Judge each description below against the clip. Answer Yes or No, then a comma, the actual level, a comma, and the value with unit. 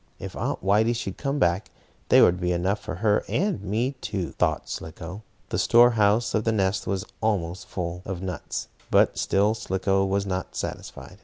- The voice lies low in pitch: Yes, low, 100 Hz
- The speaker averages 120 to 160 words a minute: No, average, 180 wpm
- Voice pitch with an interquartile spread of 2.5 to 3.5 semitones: Yes, average, 3.0 semitones